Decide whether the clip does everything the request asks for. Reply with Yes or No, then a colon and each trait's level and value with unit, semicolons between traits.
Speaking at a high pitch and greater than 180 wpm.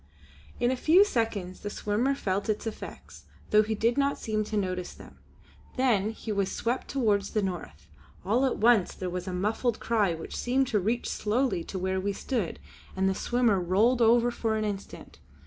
Yes: high, 215 Hz; average, 190 wpm